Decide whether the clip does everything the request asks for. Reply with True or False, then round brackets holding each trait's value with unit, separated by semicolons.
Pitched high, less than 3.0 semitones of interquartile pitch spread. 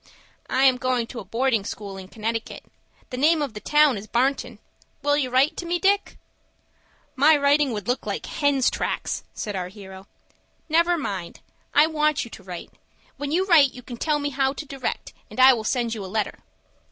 False (260 Hz; 5.1 semitones)